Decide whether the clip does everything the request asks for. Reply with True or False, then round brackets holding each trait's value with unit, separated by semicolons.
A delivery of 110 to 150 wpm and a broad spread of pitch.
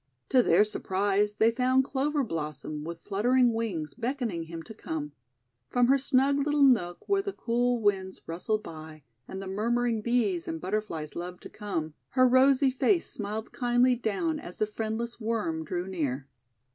False (165 wpm; 6.1 semitones)